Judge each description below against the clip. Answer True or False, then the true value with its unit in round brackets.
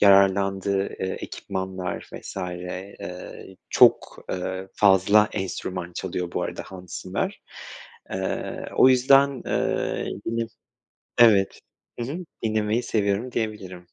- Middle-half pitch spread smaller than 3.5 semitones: True (2.6 semitones)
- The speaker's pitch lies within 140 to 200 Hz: False (95 Hz)